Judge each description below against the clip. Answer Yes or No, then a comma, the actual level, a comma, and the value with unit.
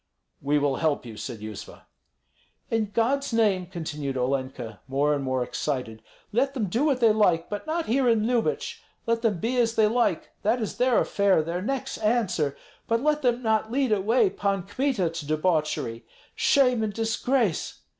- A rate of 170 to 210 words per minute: Yes, average, 175 wpm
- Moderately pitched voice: No, high, 210 Hz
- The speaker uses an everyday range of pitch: No, wide, 7.8 semitones